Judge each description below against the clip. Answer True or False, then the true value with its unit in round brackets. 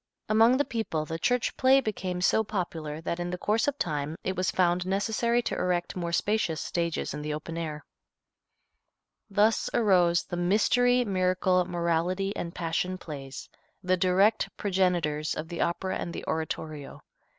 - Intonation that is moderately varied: True (3.8 semitones)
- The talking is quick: False (160 wpm)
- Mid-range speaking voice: True (180 Hz)